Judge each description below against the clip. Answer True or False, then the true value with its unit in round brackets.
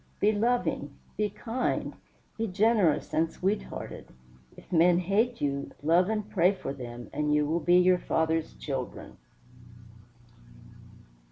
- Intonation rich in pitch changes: True (5.7 semitones)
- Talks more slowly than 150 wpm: True (135 wpm)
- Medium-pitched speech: True (175 Hz)